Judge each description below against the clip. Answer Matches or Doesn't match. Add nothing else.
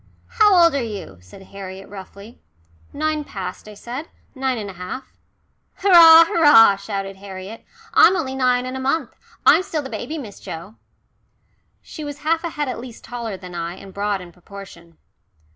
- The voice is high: Matches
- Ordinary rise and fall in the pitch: Doesn't match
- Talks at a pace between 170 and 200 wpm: Matches